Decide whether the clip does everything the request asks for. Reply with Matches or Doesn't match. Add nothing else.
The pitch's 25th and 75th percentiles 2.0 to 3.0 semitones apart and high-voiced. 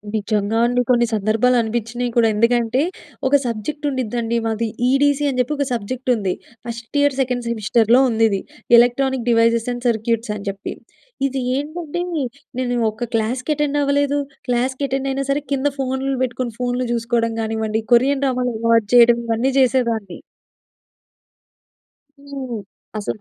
Matches